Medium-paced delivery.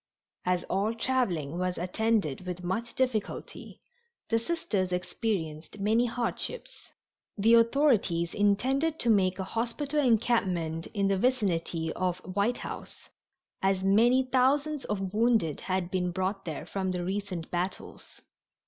No: slow, 130 wpm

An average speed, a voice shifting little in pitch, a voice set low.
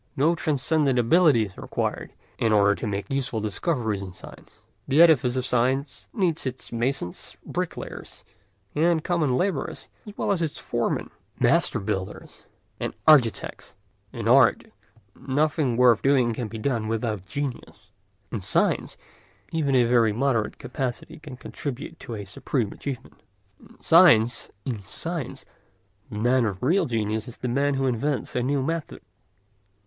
No: average, 145 wpm; average, 4.5 semitones; low, 125 Hz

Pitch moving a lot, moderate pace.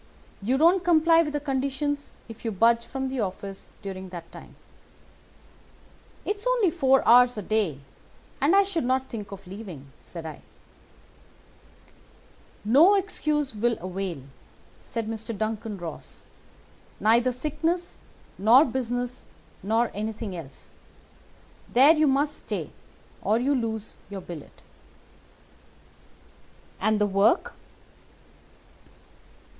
No: wide, 6.0 semitones; slow, 115 wpm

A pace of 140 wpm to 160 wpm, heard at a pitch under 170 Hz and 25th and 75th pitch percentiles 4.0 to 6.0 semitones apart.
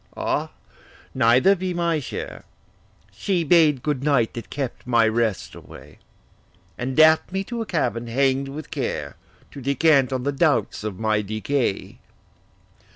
Yes: average, 145 wpm; low, 135 Hz; average, 5.2 semitones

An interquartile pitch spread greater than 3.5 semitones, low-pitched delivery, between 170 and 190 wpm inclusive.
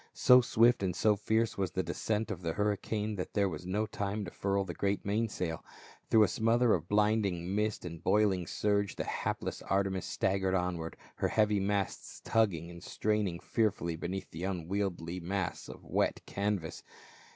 No: average, 2.9 semitones; low, 100 Hz; average, 175 wpm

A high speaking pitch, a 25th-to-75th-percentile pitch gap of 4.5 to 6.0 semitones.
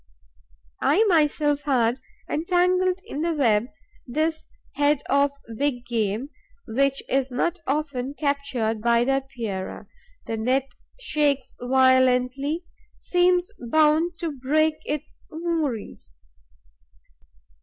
No: very high, 280 Hz; average, 4.0 semitones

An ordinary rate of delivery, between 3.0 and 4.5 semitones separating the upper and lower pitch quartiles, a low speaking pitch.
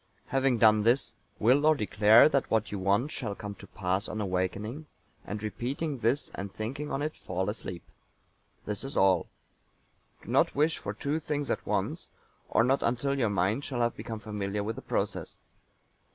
No: average, 180 wpm; average, 5.1 semitones; low, 110 Hz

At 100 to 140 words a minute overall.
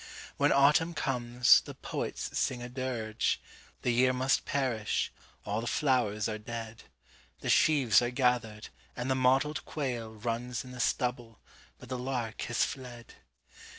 Yes: slow, 135 wpm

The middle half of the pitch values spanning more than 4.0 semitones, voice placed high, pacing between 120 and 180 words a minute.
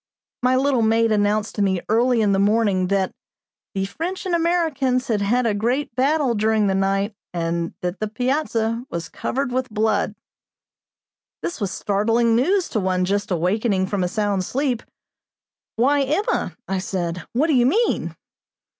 Yes: average, 4.6 semitones; high, 220 Hz; average, 165 wpm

